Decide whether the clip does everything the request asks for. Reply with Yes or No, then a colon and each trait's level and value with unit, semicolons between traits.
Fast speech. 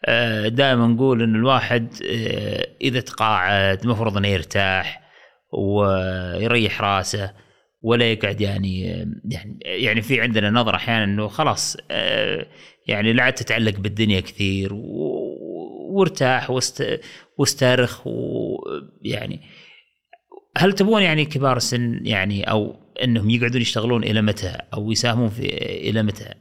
No: average, 105 wpm